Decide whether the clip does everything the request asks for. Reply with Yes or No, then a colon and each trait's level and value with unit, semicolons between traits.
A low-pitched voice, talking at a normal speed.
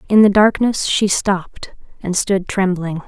No: high, 195 Hz; average, 155 wpm